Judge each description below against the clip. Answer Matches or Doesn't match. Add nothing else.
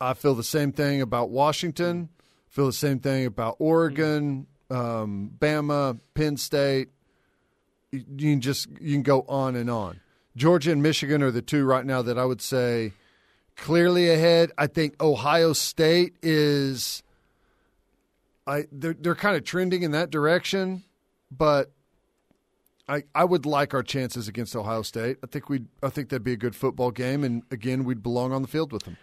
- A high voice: Doesn't match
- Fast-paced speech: Doesn't match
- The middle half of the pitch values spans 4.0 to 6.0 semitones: Doesn't match